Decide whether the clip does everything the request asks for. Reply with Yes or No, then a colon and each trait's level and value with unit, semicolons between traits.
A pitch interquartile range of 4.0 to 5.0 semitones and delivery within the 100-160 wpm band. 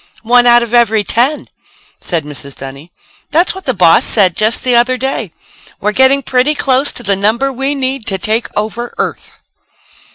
No: average, 4.5 semitones; average, 175 wpm